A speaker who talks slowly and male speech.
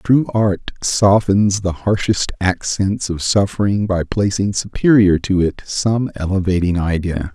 Yes: slow, 130 wpm; male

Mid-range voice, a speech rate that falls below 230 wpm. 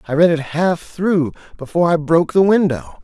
Yes: medium, 160 Hz; average, 200 wpm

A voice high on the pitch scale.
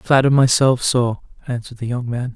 No: low, 125 Hz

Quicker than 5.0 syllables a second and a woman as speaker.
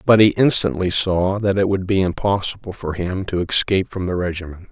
No: 5.5 syllables/s; male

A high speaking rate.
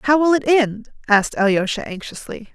No: average, 165 wpm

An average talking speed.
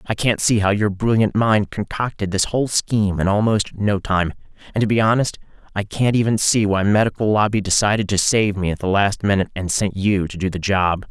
No: fast, 220 wpm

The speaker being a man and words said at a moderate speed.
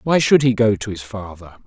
No: male; fast, 255 wpm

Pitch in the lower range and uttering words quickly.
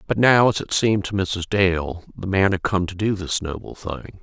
Yes: very low, 95 Hz; fast, 240 wpm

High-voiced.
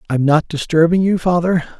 No: medium, 165 Hz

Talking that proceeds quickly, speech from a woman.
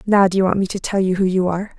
Yes: fast, 370 wpm; female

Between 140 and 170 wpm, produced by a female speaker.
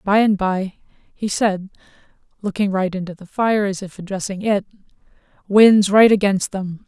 Yes: average, 155 wpm; female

